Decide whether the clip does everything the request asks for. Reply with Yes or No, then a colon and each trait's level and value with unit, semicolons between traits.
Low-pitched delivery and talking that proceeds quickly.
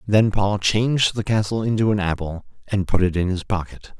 Yes: low, 100 Hz; fast, 210 wpm